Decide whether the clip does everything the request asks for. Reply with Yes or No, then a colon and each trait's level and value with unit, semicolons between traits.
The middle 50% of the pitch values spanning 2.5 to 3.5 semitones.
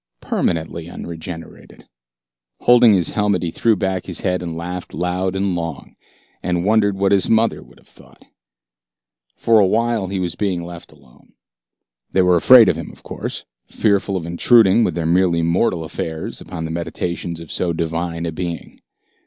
Yes: average, 2.8 semitones